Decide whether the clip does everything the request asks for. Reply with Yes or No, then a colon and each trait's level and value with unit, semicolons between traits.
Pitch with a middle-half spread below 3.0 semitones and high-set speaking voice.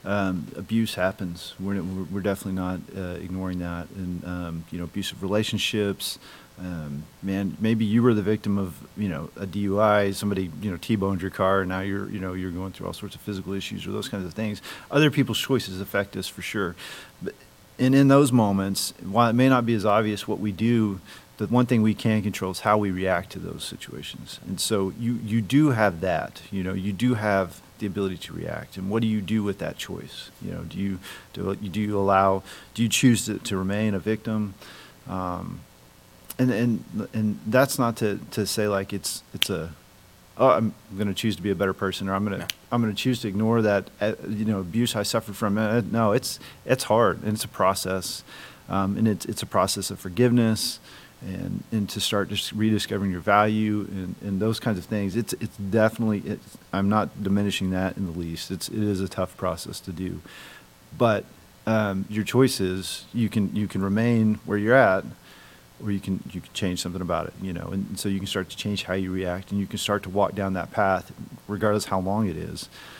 No: narrow, 2.4 semitones; low, 100 Hz